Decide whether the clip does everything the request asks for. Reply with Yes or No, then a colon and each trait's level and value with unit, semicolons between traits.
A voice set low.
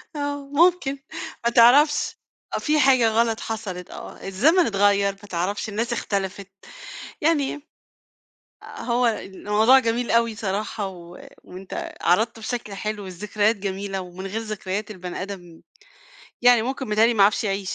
No: high, 215 Hz